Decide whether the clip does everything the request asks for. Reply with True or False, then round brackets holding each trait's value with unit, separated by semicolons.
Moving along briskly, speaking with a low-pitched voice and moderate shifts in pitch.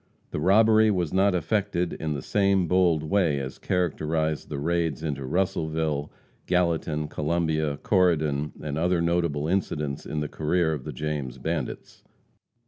False (140 wpm; 80 Hz; 3.1 semitones)